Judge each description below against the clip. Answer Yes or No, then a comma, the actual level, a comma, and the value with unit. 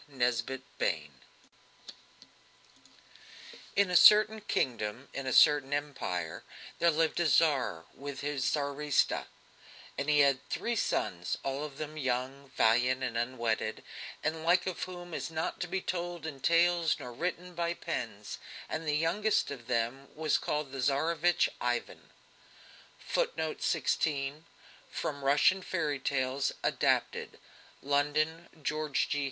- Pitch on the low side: No, medium, 145 Hz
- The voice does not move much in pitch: No, average, 4.0 semitones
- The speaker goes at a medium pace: No, slow, 130 wpm